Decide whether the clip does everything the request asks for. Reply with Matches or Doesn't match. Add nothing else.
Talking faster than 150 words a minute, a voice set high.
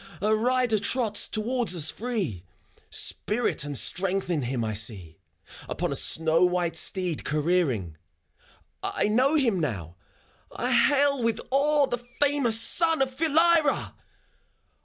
Doesn't match